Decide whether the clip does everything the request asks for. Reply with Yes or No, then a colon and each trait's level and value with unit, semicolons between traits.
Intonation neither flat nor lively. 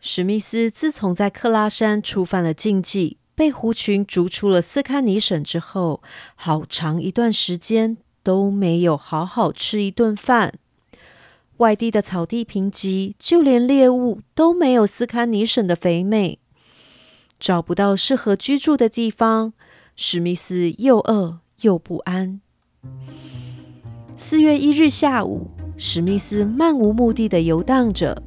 Yes: average, 4.9 semitones